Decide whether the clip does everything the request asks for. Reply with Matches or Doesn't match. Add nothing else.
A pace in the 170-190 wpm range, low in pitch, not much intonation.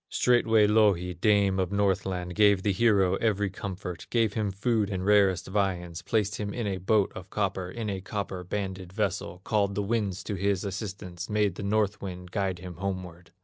Matches